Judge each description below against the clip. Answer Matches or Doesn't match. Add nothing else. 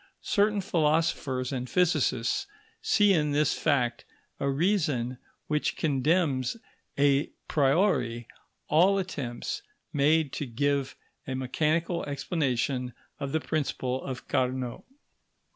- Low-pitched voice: Doesn't match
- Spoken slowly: Matches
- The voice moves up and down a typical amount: Matches